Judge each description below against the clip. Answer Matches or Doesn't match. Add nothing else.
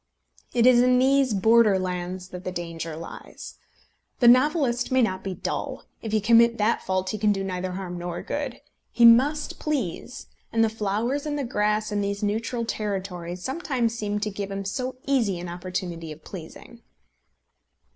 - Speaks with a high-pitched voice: Matches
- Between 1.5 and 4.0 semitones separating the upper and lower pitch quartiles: Doesn't match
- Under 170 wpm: Doesn't match